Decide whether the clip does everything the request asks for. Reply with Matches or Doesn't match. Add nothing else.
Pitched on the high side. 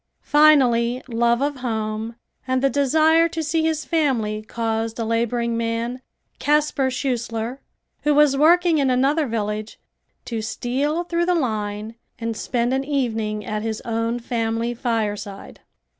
Matches